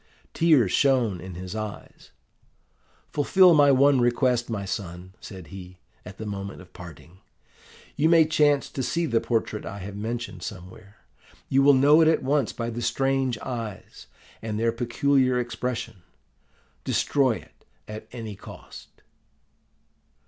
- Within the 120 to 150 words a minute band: Yes, average, 140 wpm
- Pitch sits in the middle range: No, low, 115 Hz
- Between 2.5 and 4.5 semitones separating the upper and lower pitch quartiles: No, average, 5.3 semitones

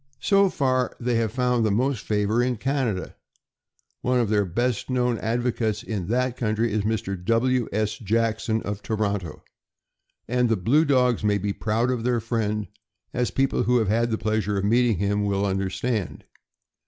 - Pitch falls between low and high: No, low, 115 Hz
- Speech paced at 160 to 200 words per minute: Yes, average, 170 wpm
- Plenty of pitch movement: No, average, 3.1 semitones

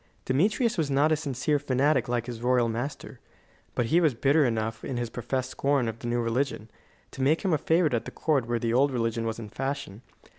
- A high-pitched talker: No, low, 130 Hz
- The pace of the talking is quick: Yes, fast, 220 wpm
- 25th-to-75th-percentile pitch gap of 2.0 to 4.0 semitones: Yes, average, 3.6 semitones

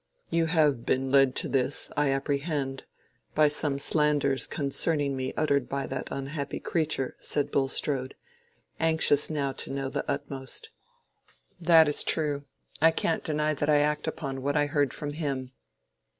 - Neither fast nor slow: Yes, average, 150 wpm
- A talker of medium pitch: Yes, medium, 145 Hz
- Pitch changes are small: Yes, narrow, 2.0 semitones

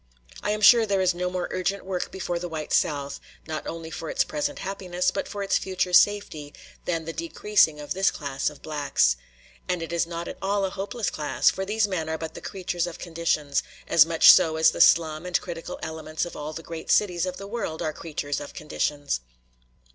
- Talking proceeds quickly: Yes, fast, 215 wpm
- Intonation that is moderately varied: Yes, average, 3.5 semitones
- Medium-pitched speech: Yes, medium, 170 Hz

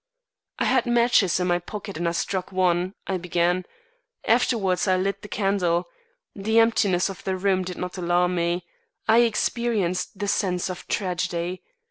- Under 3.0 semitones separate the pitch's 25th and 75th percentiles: Yes, narrow, 2.4 semitones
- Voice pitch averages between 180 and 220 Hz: Yes, medium, 185 Hz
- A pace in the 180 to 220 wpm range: No, average, 160 wpm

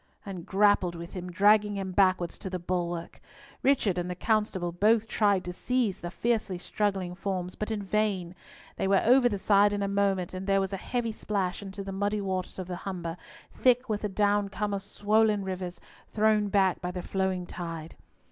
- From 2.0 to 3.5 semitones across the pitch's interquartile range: Yes, narrow, 2.4 semitones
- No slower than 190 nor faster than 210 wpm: Yes, average, 195 wpm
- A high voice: Yes, high, 195 Hz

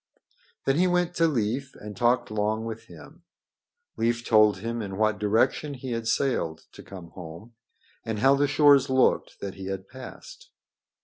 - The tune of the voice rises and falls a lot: No, average, 4.6 semitones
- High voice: No, low, 115 Hz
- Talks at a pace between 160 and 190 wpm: Yes, average, 170 wpm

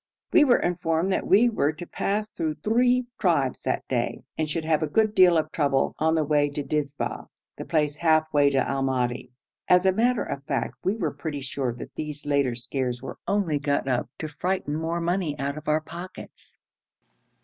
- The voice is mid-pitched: Yes, medium, 155 Hz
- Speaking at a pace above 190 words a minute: Yes, average, 200 wpm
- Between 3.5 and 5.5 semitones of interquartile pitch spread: Yes, average, 4.0 semitones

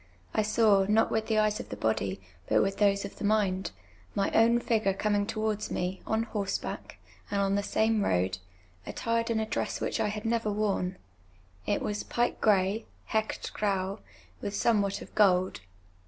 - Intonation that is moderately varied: No, narrow, 2.0 semitones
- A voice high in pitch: Yes, high, 210 Hz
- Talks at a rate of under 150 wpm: No, average, 185 wpm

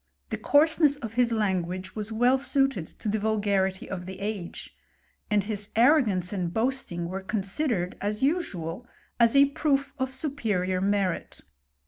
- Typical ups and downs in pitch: No, wide, 5.7 semitones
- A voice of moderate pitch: No, high, 215 Hz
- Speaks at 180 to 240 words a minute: No, average, 150 wpm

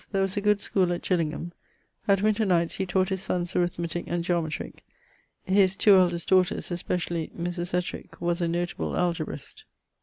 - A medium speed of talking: Yes, average, 170 wpm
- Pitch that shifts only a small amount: Yes, narrow, 1.8 semitones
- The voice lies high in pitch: No, medium, 175 Hz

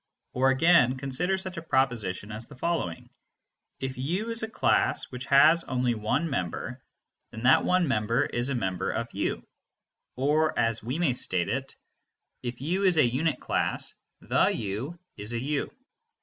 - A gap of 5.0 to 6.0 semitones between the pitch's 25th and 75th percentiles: Yes, wide, 5.6 semitones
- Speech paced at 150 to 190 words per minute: Yes, average, 165 wpm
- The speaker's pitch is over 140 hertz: No, low, 130 Hz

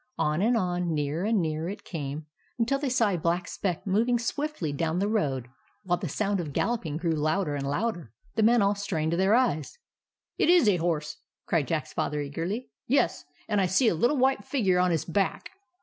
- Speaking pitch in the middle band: Yes, medium, 180 Hz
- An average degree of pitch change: No, wide, 5.8 semitones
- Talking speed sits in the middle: No, fast, 210 wpm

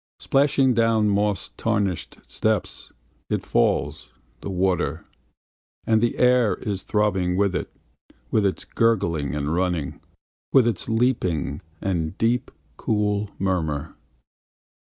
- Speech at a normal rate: No, slow, 110 wpm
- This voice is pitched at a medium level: No, low, 100 Hz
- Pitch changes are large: No, average, 4.3 semitones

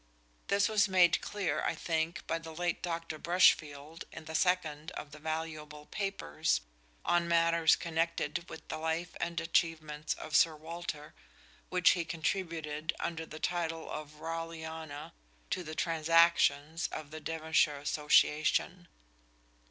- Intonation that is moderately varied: No, narrow, 1.7 semitones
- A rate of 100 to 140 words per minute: Yes, slow, 135 wpm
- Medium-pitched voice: Yes, medium, 160 Hz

